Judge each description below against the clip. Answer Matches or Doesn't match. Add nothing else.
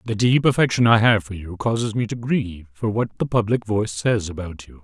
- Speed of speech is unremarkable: Doesn't match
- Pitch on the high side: Doesn't match